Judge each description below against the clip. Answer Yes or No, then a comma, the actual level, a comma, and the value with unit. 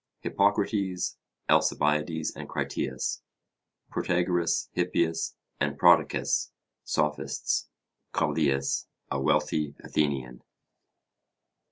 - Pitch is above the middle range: No, very low, 80 Hz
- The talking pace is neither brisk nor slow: No, slow, 65 wpm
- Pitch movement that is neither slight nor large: Yes, average, 3.8 semitones